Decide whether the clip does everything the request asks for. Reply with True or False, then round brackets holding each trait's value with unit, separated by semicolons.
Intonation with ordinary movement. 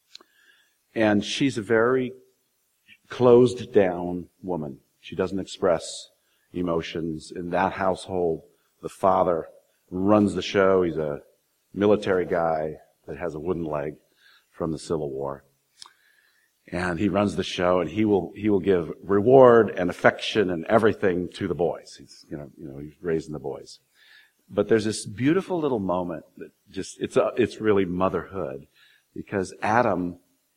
True (4.1 semitones)